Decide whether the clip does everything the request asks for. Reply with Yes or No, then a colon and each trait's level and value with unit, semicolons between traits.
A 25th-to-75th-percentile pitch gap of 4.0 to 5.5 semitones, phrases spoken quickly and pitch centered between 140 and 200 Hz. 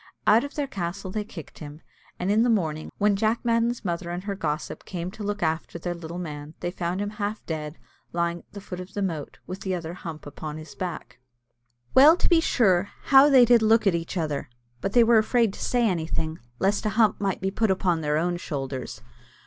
Yes: average, 4.7 semitones; fast, 225 wpm; medium, 185 Hz